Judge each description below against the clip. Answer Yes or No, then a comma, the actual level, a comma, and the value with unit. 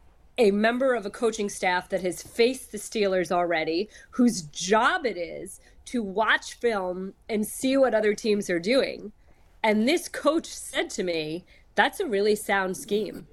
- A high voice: Yes, high, 210 Hz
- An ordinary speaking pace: Yes, average, 165 wpm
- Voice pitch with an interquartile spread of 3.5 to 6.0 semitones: Yes, average, 4.2 semitones